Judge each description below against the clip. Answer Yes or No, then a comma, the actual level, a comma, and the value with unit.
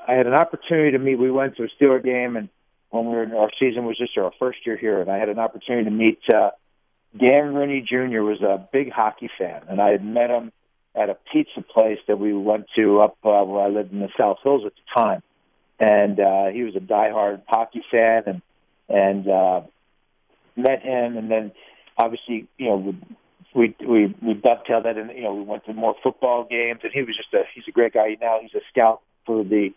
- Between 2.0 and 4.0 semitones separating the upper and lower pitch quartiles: Yes, average, 3.2 semitones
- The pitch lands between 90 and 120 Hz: Yes, low, 115 Hz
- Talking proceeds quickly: Yes, fast, 230 wpm